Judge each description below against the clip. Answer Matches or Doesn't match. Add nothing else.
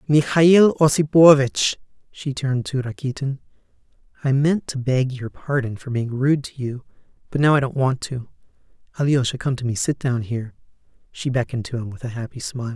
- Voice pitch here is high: Doesn't match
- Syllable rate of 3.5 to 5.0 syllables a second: Doesn't match